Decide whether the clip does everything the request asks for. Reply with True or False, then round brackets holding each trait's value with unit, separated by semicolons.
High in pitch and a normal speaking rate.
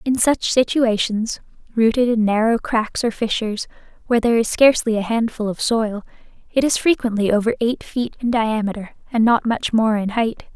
True (225 Hz; 175 wpm)